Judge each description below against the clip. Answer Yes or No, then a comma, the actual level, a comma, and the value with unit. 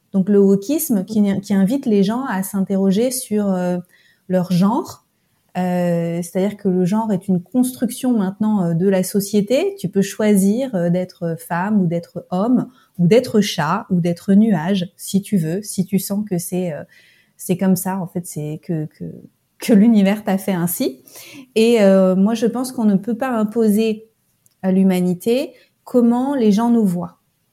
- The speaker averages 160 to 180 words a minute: Yes, average, 175 wpm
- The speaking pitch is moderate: No, high, 195 Hz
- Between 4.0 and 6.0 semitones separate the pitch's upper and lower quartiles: No, average, 3.4 semitones